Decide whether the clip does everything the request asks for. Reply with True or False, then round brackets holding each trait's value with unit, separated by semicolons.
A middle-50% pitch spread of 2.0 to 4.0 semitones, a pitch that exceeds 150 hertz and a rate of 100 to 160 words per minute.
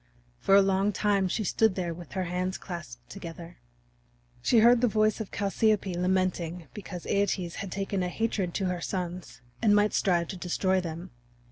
False (2.4 semitones; 185 Hz; 175 wpm)